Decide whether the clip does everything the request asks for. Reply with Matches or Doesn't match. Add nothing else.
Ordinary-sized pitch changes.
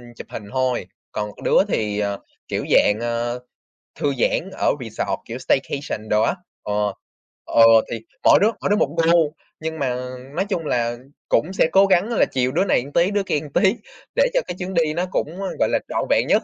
Doesn't match